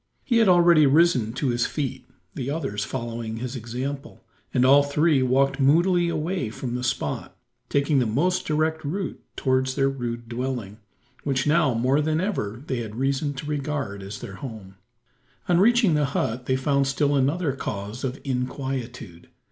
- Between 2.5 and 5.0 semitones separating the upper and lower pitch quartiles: Yes, average, 3.8 semitones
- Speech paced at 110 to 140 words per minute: No, average, 165 wpm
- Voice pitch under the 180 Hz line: Yes, low, 135 Hz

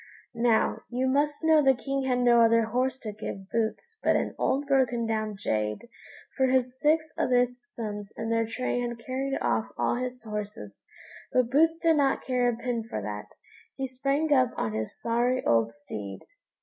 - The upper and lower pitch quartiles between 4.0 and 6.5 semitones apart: No, average, 3.3 semitones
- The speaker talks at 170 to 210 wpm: Yes, average, 180 wpm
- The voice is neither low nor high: No, high, 245 Hz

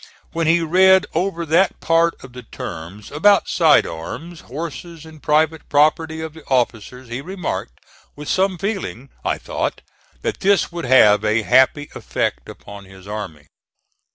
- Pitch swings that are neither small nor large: No, wide, 6.6 semitones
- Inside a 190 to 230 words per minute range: No, average, 155 wpm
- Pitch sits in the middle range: Yes, medium, 155 Hz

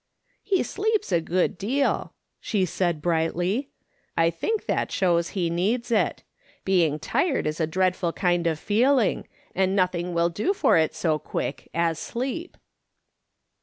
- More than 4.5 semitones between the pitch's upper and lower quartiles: Yes, wide, 5.6 semitones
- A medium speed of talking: Yes, average, 160 wpm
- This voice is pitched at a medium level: Yes, medium, 180 Hz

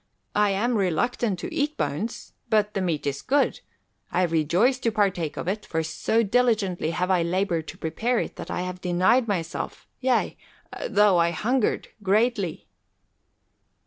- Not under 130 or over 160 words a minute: Yes, average, 155 wpm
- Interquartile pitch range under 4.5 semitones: No, average, 5.1 semitones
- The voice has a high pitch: Yes, high, 195 Hz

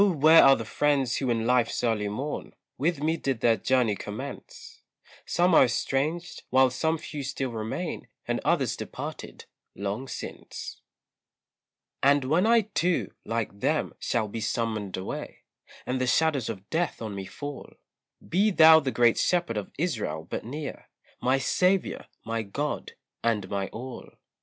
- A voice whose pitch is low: Yes, low, 130 Hz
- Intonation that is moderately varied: No, wide, 5.9 semitones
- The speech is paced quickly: No, average, 150 wpm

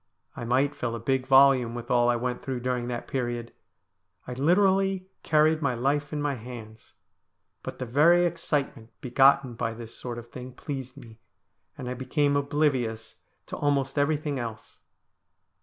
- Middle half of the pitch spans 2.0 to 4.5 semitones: Yes, average, 3.3 semitones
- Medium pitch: No, low, 130 Hz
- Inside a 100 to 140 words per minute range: No, average, 160 wpm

